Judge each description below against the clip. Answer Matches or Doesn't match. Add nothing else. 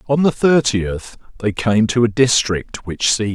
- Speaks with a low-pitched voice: Matches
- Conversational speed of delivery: Matches